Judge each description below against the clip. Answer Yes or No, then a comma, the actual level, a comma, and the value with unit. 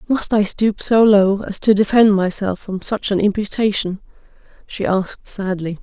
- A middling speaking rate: Yes, average, 165 wpm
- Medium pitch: No, high, 200 Hz